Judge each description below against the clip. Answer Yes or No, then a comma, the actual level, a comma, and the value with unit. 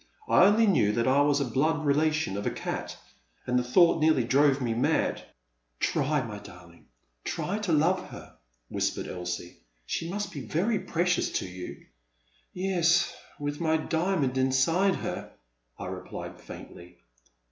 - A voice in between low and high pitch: Yes, medium, 145 Hz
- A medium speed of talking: Yes, average, 155 wpm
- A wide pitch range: Yes, wide, 6.2 semitones